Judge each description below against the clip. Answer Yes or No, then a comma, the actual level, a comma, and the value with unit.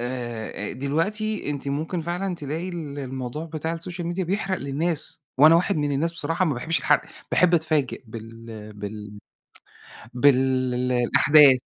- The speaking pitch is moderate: Yes, medium, 145 Hz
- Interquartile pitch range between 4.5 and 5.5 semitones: Yes, average, 5.0 semitones